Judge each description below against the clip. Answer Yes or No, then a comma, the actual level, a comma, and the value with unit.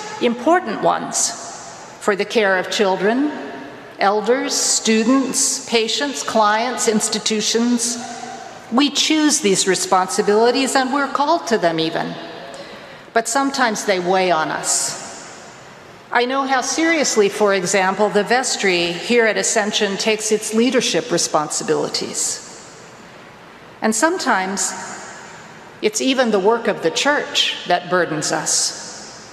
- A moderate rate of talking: No, slow, 115 wpm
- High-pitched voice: Yes, high, 220 Hz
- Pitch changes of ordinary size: Yes, average, 4.9 semitones